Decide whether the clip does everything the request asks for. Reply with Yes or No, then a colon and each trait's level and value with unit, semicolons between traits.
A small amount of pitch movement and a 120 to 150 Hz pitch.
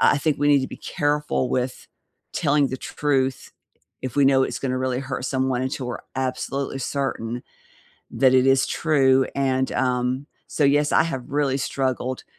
Yes: narrow, 1.5 semitones; low, 135 Hz